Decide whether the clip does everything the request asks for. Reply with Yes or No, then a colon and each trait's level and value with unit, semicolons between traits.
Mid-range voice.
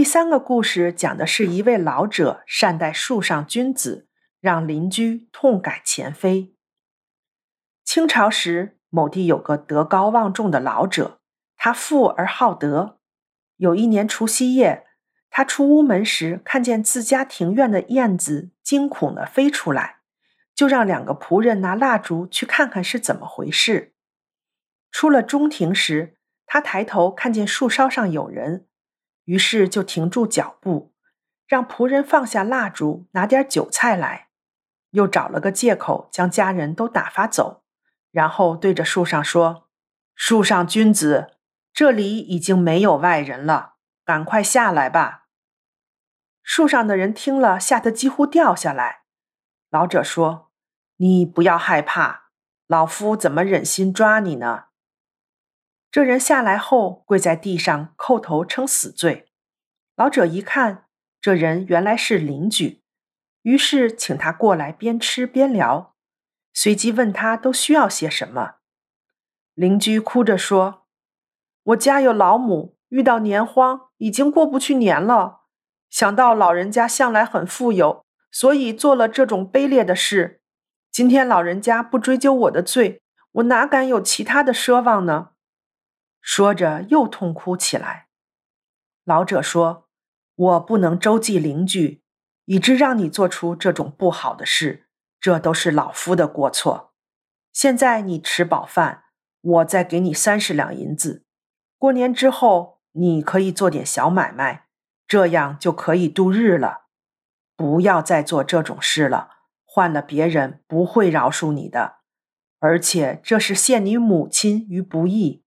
No: high, 205 Hz